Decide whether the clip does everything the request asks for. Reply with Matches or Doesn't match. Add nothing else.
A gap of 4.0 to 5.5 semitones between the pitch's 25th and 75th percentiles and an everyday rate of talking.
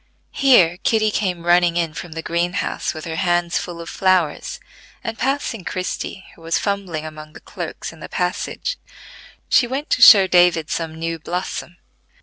Doesn't match